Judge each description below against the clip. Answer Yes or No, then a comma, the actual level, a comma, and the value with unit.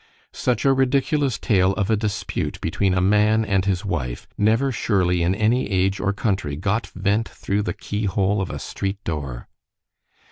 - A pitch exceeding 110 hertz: No, low, 100 Hz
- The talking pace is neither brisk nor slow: Yes, average, 175 wpm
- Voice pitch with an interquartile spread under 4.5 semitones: Yes, average, 2.8 semitones